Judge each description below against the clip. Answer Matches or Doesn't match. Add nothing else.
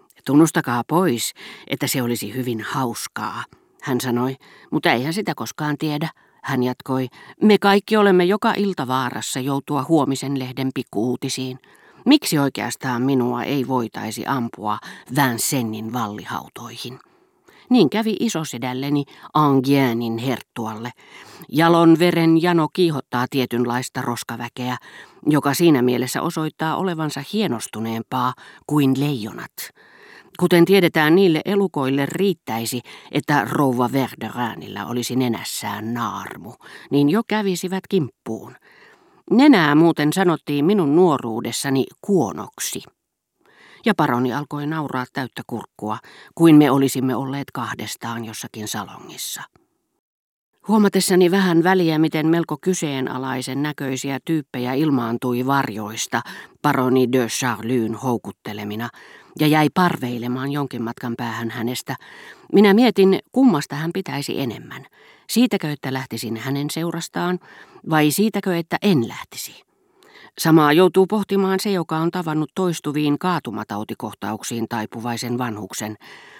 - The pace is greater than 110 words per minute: Doesn't match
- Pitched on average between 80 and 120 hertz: Doesn't match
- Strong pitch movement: Matches